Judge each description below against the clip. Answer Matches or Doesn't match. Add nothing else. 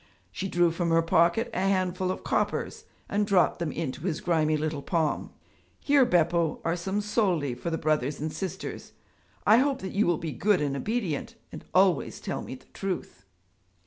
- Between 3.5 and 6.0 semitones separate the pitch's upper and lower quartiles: Matches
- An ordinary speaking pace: Matches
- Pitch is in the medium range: Matches